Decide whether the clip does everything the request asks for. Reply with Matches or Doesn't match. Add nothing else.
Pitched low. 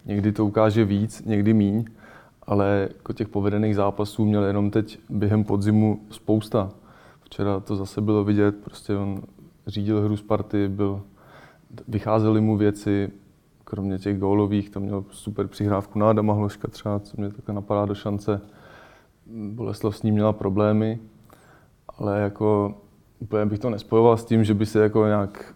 Matches